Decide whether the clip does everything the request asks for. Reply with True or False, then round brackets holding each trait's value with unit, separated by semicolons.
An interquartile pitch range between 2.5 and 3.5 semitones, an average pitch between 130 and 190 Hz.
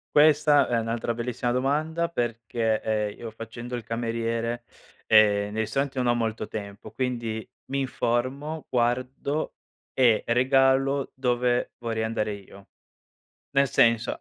False (2.8 semitones; 120 Hz)